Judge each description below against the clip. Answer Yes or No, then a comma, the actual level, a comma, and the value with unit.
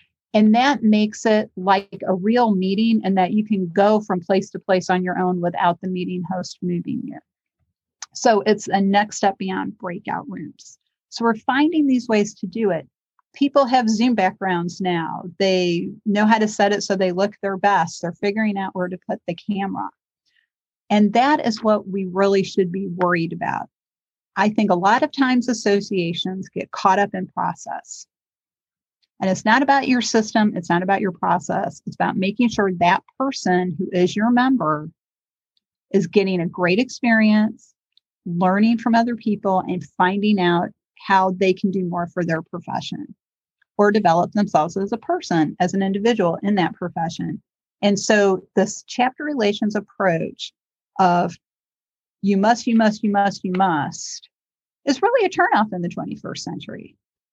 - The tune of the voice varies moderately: Yes, average, 3.3 semitones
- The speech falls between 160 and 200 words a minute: Yes, average, 175 wpm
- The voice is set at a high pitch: Yes, high, 200 Hz